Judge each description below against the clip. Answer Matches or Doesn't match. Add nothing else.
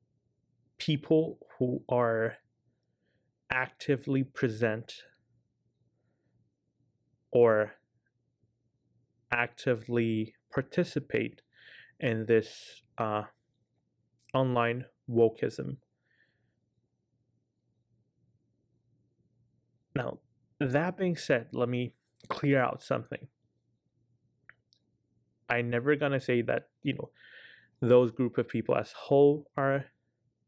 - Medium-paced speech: Doesn't match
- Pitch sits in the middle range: Doesn't match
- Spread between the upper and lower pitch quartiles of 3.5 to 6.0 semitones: Doesn't match